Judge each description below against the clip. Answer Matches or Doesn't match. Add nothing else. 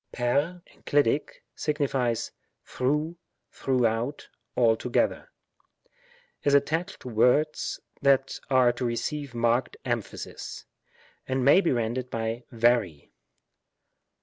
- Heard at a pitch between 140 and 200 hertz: Doesn't match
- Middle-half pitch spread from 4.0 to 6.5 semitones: Doesn't match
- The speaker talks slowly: Matches